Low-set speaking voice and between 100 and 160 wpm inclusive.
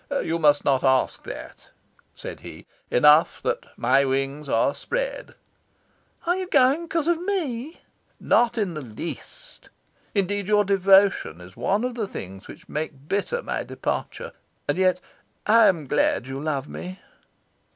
No: medium, 185 Hz; average, 150 wpm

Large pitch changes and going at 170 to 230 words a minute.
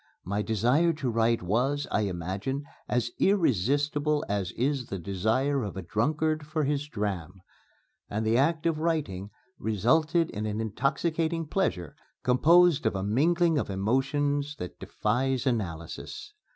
No: wide, 6.7 semitones; average, 140 wpm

